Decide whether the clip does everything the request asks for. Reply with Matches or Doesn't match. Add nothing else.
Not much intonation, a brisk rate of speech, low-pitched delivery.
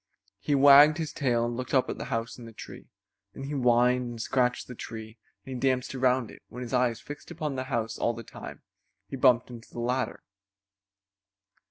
Matches